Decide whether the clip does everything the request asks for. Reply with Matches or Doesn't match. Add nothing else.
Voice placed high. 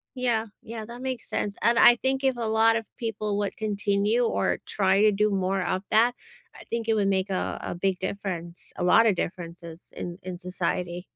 Matches